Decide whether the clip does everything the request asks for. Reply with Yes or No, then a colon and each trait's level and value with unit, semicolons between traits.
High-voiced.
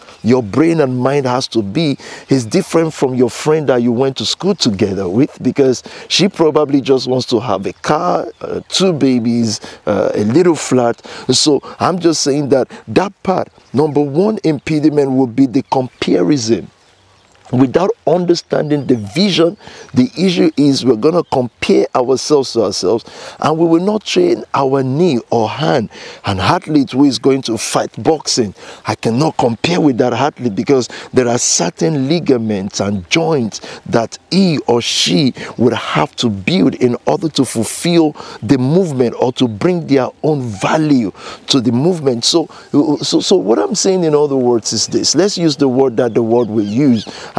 No: low, 135 Hz